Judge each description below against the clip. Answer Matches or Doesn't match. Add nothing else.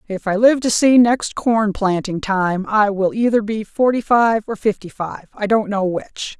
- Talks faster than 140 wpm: Matches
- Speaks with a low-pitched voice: Doesn't match